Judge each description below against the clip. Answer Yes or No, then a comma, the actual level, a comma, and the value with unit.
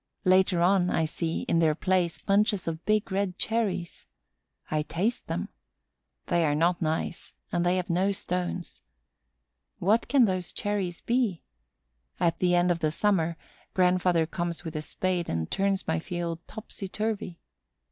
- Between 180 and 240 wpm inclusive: No, average, 155 wpm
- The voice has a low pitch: No, medium, 180 Hz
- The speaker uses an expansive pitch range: No, average, 2.7 semitones